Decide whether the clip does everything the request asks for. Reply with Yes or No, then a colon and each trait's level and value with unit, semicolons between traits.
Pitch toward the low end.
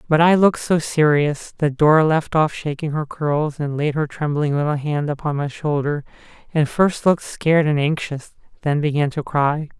No: medium, 150 Hz